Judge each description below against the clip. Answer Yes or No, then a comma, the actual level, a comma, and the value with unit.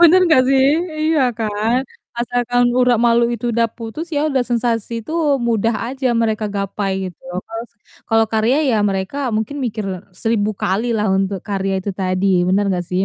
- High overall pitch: Yes, high, 225 Hz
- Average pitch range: Yes, average, 3.3 semitones